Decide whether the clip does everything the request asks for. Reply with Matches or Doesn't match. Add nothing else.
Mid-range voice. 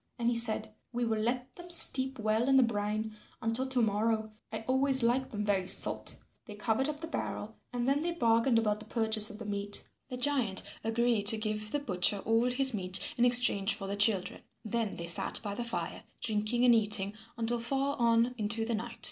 Doesn't match